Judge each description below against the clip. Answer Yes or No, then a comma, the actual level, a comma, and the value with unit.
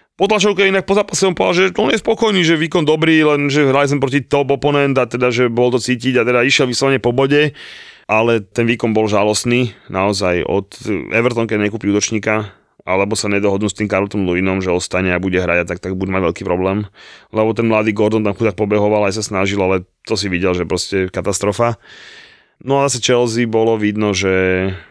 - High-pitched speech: No, low, 110 Hz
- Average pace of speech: No, fast, 210 wpm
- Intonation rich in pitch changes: Yes, wide, 5.7 semitones